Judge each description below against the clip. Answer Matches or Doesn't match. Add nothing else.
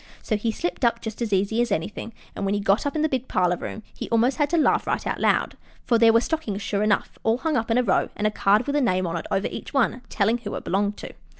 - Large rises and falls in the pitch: Doesn't match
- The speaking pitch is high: Matches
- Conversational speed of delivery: Doesn't match